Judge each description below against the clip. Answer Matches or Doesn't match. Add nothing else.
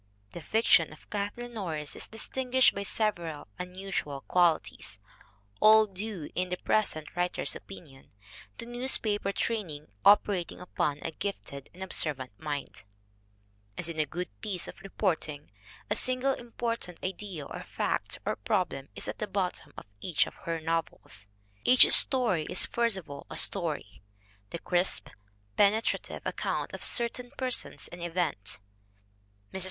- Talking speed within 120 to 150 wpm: Matches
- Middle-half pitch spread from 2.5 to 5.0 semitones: Doesn't match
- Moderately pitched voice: Matches